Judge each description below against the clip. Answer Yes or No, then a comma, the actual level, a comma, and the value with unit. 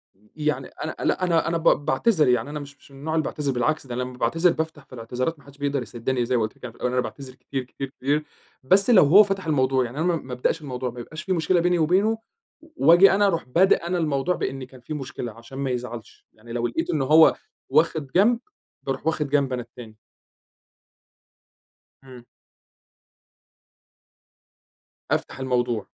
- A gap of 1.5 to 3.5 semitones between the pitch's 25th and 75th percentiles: No, average, 4.5 semitones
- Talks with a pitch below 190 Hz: Yes, medium, 140 Hz